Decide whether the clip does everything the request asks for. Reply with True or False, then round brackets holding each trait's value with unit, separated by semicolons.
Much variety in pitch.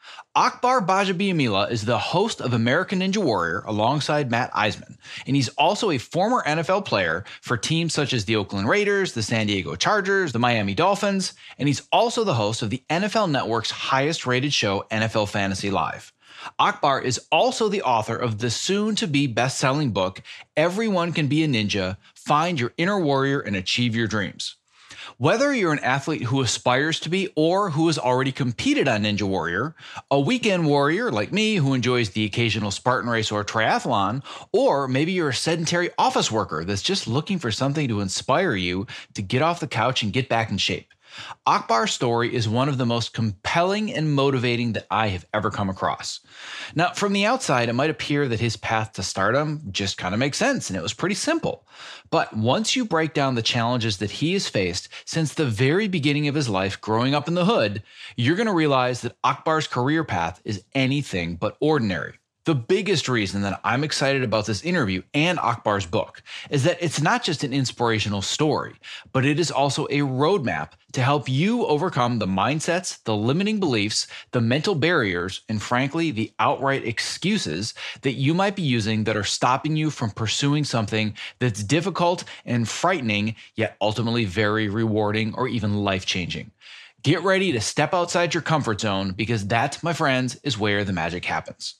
True (6.3 semitones)